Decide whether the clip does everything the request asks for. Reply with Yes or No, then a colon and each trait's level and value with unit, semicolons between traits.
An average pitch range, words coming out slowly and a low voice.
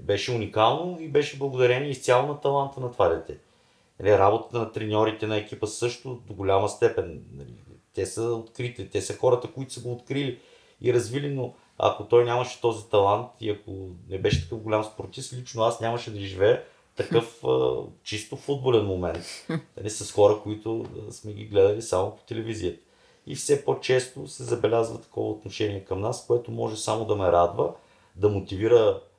No: average, 3.6 semitones; fast, 165 wpm; low, 115 Hz